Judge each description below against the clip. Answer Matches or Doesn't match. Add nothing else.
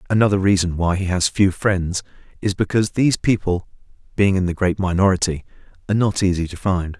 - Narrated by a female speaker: Doesn't match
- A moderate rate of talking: Matches